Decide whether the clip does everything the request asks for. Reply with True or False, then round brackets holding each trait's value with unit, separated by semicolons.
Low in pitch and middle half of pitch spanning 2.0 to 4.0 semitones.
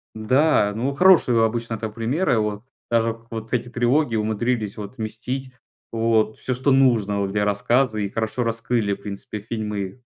True (115 Hz; 2.6 semitones)